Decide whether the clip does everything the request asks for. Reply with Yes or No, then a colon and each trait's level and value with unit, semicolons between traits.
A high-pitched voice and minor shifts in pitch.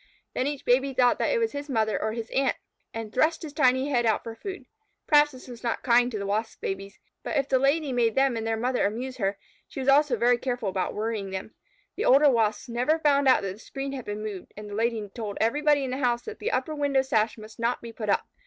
No: high, 245 Hz; average, 3.9 semitones